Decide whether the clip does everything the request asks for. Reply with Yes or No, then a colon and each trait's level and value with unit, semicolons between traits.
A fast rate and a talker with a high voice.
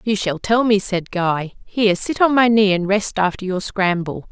Yes: fast, 220 wpm; high, 200 Hz